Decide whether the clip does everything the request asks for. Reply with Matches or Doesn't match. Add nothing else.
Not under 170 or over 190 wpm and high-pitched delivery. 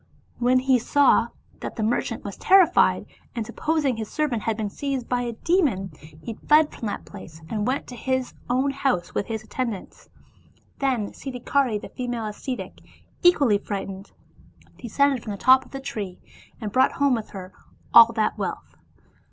Matches